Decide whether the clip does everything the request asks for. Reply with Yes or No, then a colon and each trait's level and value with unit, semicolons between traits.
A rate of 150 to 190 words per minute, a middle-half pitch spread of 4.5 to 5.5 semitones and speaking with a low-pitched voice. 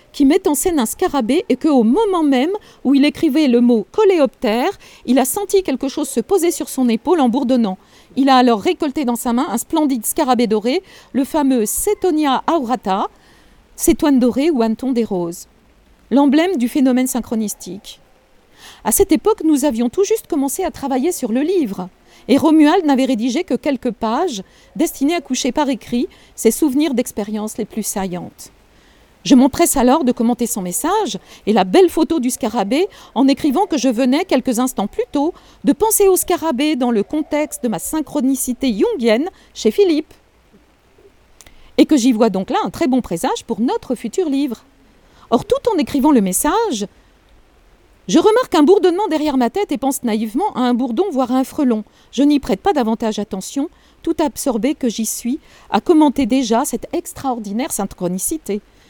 No: average, 175 wpm; average, 5.0 semitones; very high, 270 Hz